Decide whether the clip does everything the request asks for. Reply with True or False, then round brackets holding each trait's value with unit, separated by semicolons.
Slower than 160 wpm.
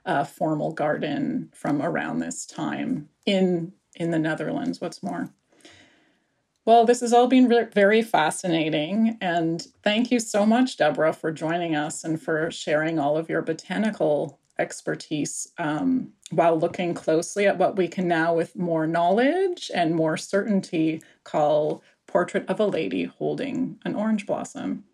True (150 wpm)